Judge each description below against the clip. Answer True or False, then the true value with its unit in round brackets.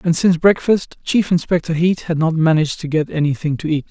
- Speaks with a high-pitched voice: False (165 Hz)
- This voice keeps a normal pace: False (215 wpm)